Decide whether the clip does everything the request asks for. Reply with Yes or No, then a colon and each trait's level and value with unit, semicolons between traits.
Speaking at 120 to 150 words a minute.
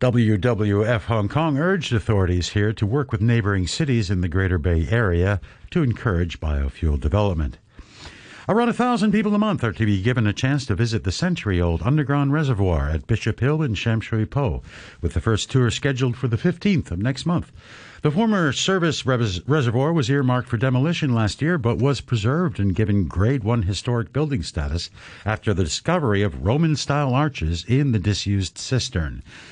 No: average, 175 wpm